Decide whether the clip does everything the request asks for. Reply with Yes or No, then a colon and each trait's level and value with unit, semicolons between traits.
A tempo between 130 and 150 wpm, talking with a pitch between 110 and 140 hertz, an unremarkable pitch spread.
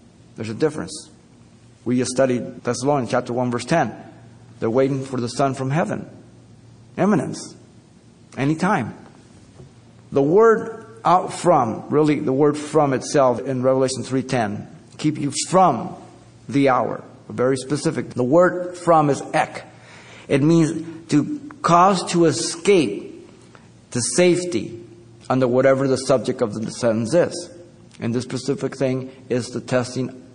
Yes: slow, 135 wpm; low, 135 Hz; average, 4.4 semitones